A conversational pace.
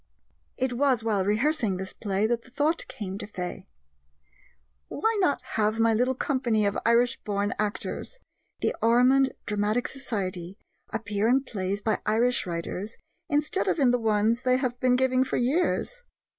Yes: average, 155 wpm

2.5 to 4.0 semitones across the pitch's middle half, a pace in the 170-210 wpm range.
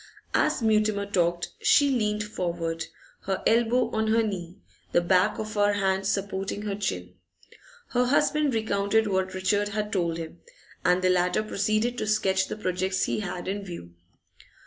No: average, 2.8 semitones; average, 160 wpm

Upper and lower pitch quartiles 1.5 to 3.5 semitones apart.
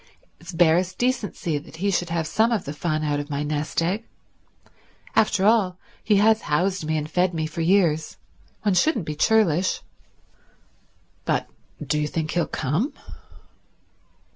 No: average, 4.6 semitones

